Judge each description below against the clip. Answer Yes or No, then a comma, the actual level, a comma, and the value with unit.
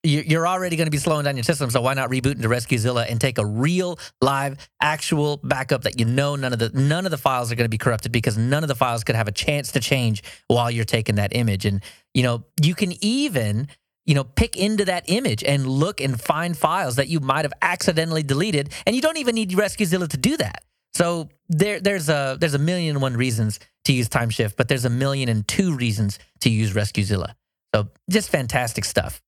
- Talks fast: Yes, fast, 230 wpm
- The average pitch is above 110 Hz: Yes, low, 135 Hz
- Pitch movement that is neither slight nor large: No, wide, 5.8 semitones